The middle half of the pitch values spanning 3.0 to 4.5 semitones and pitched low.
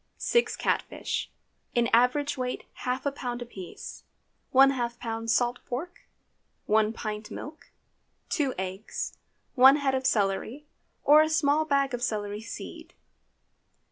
No: average, 3.9 semitones; very high, 250 Hz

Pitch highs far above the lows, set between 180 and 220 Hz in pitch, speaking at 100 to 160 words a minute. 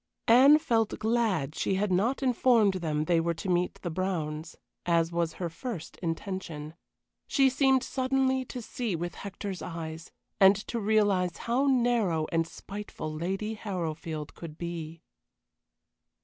Yes: wide, 5.9 semitones; high, 190 Hz; average, 140 wpm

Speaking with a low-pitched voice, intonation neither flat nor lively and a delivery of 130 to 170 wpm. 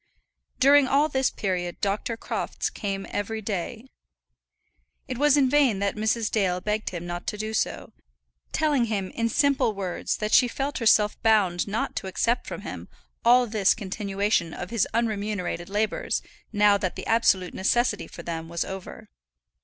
No: high, 210 Hz; average, 3.4 semitones; average, 160 wpm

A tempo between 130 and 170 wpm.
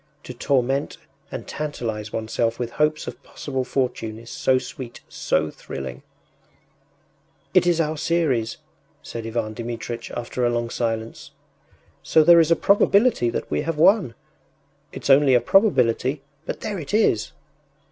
Yes: average, 145 wpm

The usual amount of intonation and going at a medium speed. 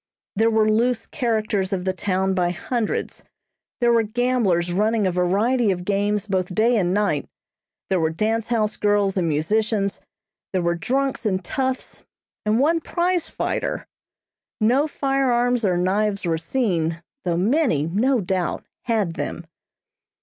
Yes: average, 4.6 semitones; average, 145 wpm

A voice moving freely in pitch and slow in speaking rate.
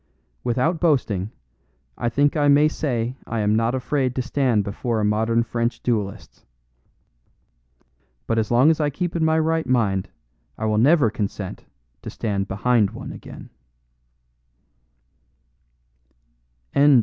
No: average, 5.0 semitones; slow, 130 wpm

